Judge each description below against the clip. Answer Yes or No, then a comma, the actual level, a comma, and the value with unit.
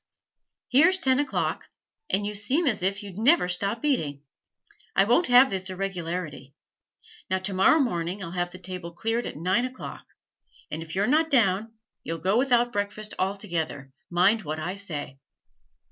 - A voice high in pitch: Yes, high, 195 Hz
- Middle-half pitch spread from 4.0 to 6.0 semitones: Yes, average, 5.3 semitones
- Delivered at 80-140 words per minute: No, average, 160 wpm